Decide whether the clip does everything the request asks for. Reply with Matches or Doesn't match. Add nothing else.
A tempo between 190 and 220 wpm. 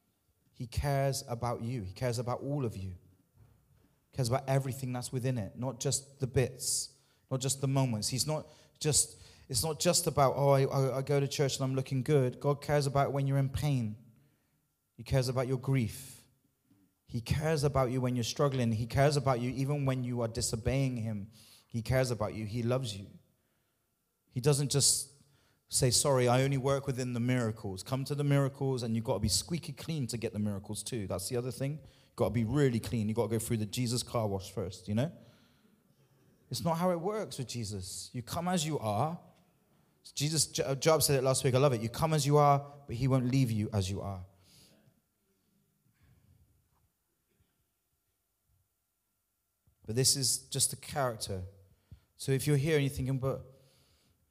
Matches